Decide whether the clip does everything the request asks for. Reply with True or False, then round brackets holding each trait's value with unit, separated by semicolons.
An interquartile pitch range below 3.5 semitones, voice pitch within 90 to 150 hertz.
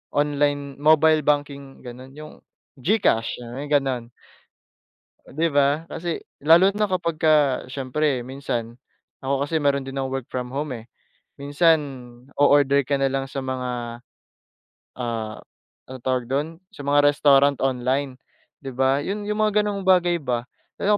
True (2.8 semitones; 140 Hz)